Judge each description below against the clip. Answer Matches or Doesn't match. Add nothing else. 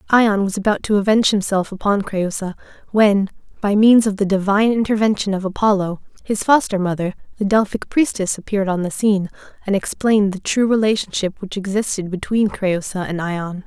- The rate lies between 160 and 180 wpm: Matches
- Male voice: Doesn't match